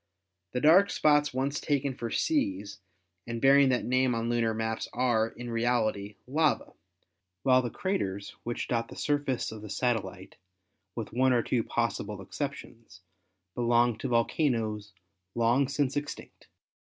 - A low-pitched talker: Yes, low, 120 Hz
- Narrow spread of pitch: No, average, 3.4 semitones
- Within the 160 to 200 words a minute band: No, average, 145 wpm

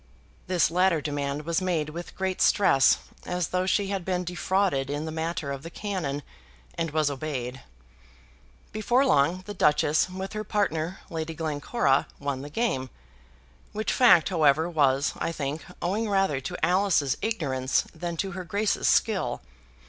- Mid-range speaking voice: Yes, medium, 165 Hz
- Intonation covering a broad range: No, average, 4.7 semitones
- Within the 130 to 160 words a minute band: Yes, average, 155 wpm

